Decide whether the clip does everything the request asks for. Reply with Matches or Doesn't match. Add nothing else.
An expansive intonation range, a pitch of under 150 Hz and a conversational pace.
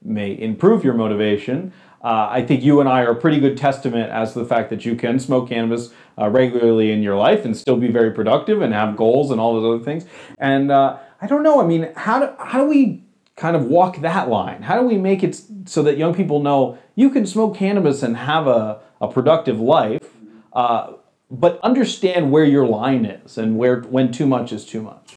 Doesn't match